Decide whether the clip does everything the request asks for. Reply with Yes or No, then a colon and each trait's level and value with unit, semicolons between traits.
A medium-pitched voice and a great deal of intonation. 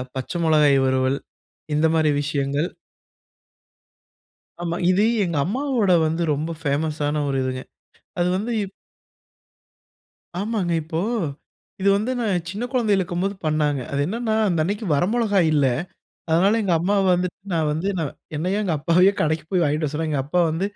No: medium, 170 Hz; average, 4.6 semitones